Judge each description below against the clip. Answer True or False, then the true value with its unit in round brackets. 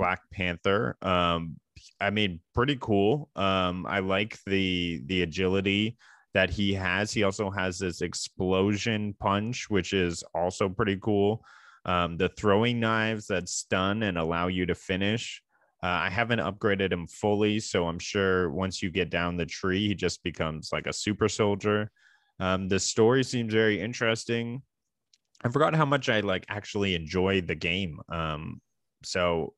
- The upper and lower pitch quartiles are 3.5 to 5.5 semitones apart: False (2.9 semitones)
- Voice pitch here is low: True (100 Hz)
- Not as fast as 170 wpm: True (160 wpm)